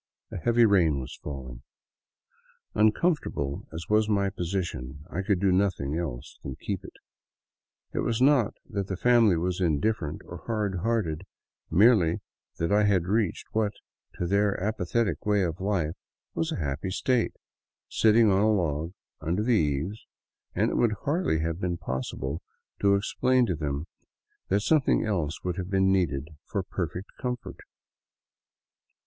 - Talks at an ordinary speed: Yes, average, 155 wpm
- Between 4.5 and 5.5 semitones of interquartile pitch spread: Yes, average, 4.9 semitones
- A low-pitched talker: Yes, very low, 95 Hz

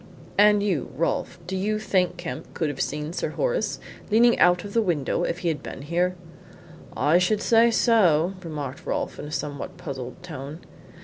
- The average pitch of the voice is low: No, medium, 175 Hz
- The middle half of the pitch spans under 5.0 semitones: No, wide, 5.4 semitones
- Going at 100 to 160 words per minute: No, average, 180 wpm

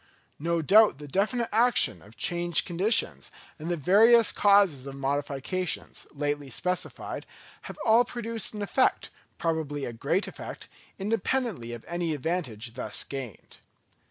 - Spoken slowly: Yes, slow, 130 wpm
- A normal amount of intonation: No, wide, 6.9 semitones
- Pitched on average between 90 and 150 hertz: No, medium, 170 Hz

